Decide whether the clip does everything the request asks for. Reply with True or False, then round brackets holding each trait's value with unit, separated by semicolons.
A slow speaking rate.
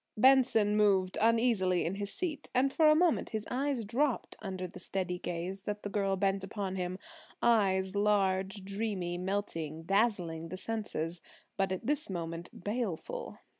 False (150 wpm)